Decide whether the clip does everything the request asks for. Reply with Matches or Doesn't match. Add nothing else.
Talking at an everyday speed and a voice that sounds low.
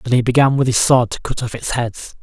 Doesn't match